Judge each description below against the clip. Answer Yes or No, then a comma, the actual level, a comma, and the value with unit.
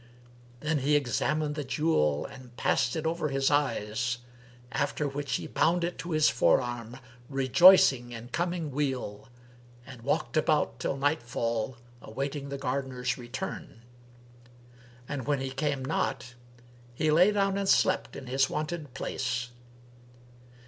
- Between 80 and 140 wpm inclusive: Yes, slow, 135 wpm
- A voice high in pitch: No, low, 135 Hz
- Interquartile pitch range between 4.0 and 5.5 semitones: No, average, 3.6 semitones